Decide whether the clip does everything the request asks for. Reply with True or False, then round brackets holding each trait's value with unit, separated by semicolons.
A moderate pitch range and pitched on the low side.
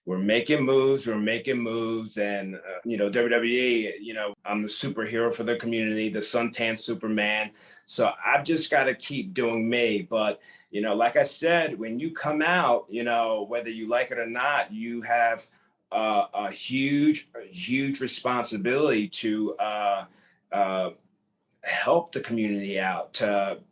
True (3.1 semitones; 115 Hz)